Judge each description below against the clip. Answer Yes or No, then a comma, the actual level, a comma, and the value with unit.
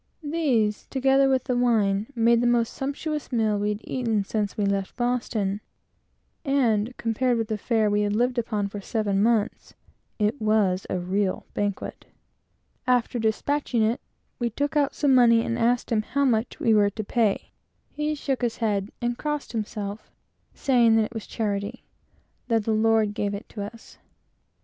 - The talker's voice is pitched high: Yes, high, 225 Hz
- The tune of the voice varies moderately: Yes, average, 3.0 semitones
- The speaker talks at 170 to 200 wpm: Yes, average, 175 wpm